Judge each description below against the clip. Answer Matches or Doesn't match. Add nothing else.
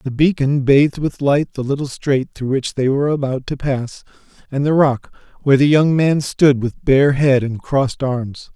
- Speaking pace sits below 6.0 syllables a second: Matches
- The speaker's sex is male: Matches